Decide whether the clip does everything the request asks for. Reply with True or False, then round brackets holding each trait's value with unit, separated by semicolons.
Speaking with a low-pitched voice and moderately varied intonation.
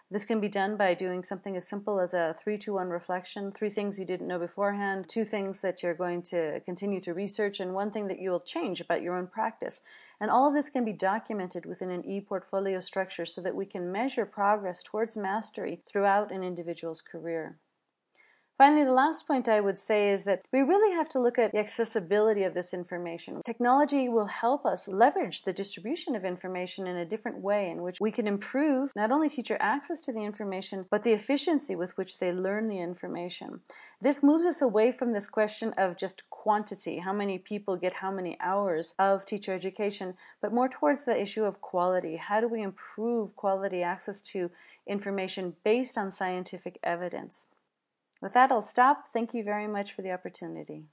False (200 Hz; 3.5 semitones)